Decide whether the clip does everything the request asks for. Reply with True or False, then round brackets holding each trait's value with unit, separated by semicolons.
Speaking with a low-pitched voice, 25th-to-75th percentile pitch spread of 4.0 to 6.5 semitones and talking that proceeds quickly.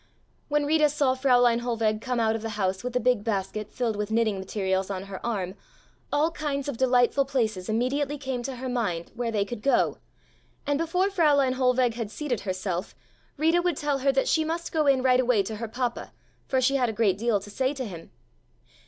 False (245 Hz; 4.4 semitones; 210 wpm)